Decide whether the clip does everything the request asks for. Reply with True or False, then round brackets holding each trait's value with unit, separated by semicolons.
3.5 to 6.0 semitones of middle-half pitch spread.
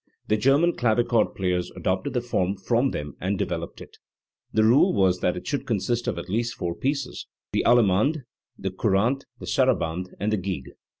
True (4.6 semitones)